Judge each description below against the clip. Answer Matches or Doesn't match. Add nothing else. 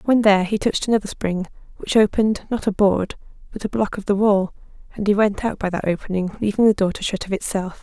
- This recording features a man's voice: Doesn't match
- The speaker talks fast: Matches